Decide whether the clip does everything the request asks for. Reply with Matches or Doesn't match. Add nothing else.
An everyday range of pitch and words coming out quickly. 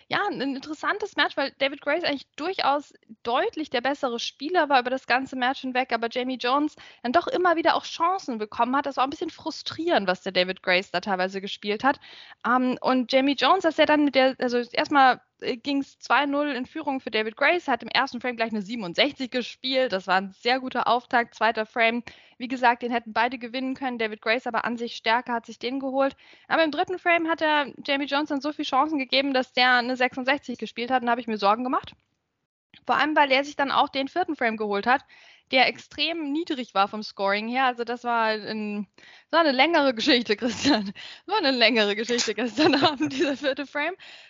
Matches